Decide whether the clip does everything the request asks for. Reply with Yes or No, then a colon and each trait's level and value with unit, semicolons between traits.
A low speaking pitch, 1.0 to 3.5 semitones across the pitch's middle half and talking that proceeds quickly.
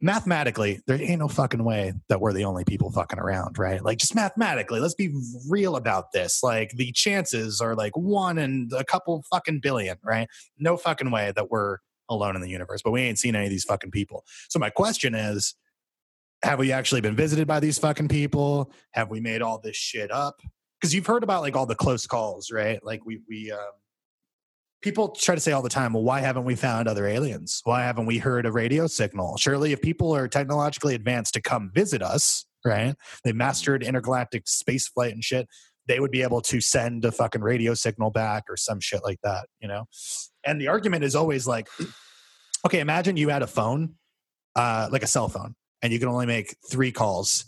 No: low, 125 Hz; average, 4.9 semitones; fast, 210 wpm